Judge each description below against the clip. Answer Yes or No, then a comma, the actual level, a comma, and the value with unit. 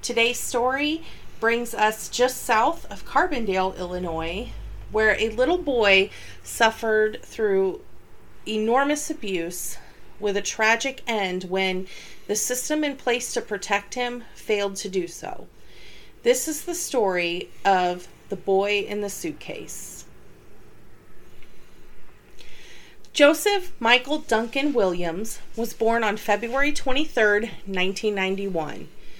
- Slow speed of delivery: Yes, slow, 110 wpm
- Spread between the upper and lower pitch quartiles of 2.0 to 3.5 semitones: No, average, 4.7 semitones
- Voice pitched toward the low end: No, high, 220 Hz